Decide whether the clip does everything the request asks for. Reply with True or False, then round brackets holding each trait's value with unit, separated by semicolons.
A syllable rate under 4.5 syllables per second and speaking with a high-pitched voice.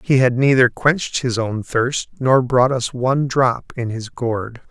False (4.0 syllables/s; 125 Hz)